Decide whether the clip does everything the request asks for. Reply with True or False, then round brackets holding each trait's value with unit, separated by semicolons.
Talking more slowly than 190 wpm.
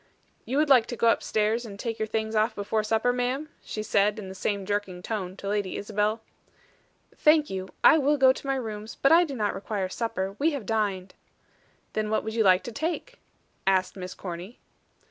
False (205 wpm)